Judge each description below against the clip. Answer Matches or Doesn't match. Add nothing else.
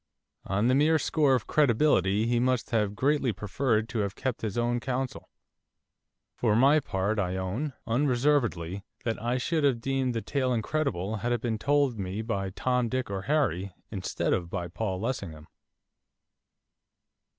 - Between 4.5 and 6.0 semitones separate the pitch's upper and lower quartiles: Matches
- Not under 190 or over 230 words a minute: Doesn't match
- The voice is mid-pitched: Doesn't match